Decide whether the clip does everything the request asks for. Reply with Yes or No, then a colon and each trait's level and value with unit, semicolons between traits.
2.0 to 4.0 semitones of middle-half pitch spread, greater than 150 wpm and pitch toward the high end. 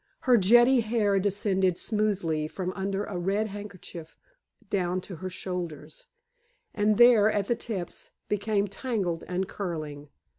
No: average, 2.9 semitones; slow, 135 wpm; high, 195 Hz